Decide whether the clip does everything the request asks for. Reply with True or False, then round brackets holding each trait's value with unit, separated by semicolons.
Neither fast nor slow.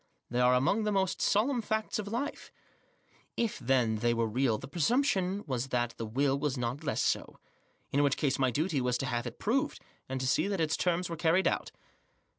False (210 wpm)